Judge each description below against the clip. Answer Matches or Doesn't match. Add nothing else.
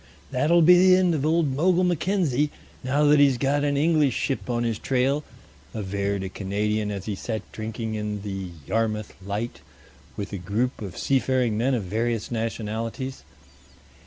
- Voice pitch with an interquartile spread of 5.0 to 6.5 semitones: Matches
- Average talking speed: Matches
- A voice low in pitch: Matches